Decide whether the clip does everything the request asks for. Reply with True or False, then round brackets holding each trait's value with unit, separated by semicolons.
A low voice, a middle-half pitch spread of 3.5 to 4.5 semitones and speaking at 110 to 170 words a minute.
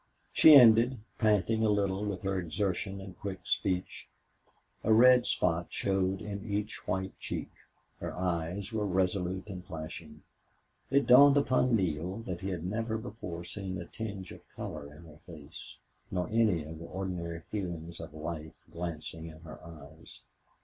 True (95 Hz; 3.8 semitones; 155 wpm)